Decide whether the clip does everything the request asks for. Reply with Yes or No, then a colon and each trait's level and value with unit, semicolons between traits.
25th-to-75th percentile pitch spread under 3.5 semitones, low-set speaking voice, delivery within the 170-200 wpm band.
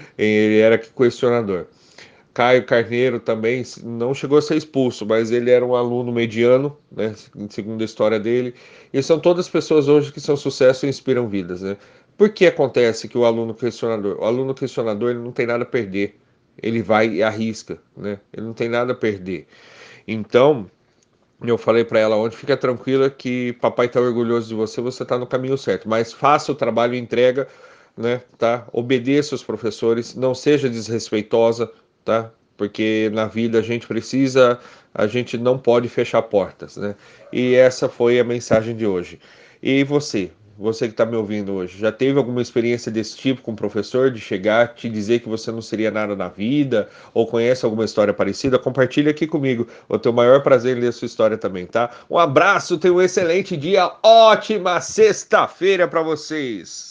Yes: average, 3.1 semitones; low, 120 Hz; average, 180 wpm